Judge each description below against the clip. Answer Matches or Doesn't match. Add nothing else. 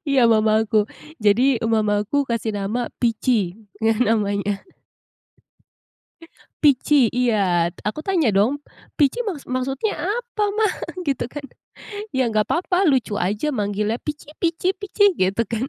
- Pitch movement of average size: Doesn't match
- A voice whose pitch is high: Matches